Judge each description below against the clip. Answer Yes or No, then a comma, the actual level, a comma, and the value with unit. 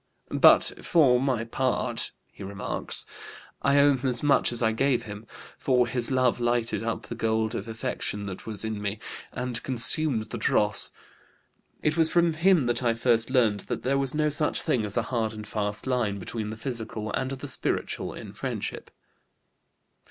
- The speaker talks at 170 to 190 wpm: Yes, average, 180 wpm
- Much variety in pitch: No, average, 3.3 semitones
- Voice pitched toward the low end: Yes, low, 120 Hz